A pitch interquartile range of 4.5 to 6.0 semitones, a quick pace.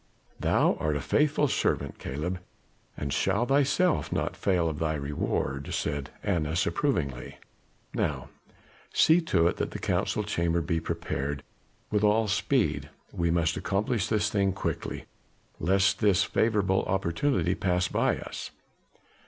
No: average, 5.2 semitones; slow, 135 wpm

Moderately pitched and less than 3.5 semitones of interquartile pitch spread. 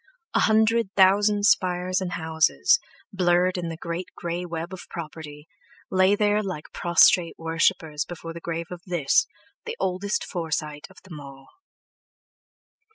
Yes: medium, 175 Hz; narrow, 2.6 semitones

